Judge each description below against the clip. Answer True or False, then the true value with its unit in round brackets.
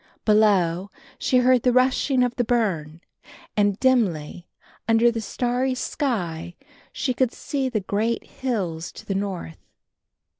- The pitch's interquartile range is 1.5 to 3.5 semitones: False (5.5 semitones)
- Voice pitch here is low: False (220 Hz)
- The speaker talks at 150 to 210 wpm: False (135 wpm)